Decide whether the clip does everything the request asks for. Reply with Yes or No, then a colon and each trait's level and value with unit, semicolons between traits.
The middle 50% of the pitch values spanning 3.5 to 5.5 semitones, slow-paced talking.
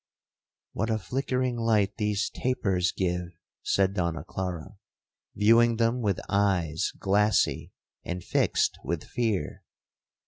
Yes: average, 4.1 semitones; slow, 110 wpm